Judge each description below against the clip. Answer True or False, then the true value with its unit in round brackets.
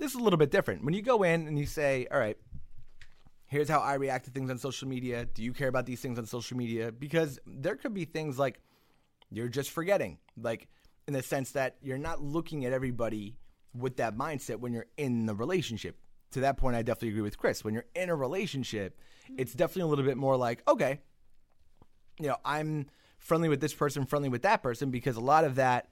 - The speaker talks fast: True (225 wpm)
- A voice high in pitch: False (135 Hz)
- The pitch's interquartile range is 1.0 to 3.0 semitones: False (3.7 semitones)